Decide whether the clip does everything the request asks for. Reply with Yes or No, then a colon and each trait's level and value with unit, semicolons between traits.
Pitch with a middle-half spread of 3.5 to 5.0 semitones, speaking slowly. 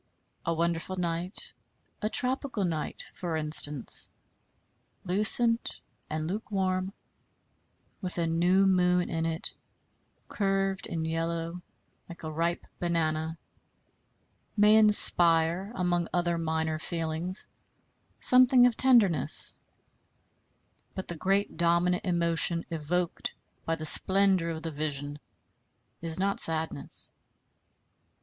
No: average, 2.8 semitones; slow, 100 wpm